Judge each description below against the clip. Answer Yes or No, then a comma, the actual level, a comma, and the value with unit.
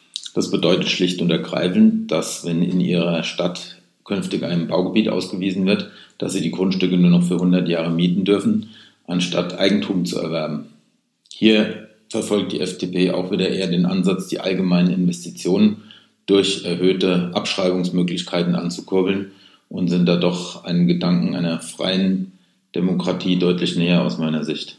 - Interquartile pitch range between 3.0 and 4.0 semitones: No, narrow, 2.5 semitones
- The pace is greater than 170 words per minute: No, average, 145 wpm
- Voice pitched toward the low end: Yes, very low, 90 Hz